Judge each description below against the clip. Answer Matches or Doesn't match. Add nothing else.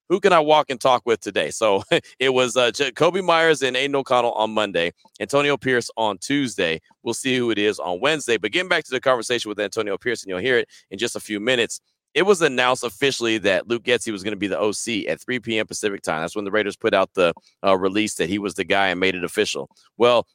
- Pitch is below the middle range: Matches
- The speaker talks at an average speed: Doesn't match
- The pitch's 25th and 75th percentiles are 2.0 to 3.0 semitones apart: Doesn't match